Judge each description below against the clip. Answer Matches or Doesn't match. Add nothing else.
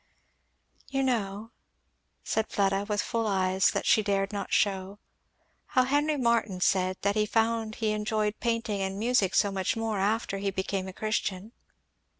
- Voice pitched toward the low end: Doesn't match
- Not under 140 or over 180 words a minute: Matches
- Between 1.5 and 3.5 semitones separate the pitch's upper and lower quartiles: Matches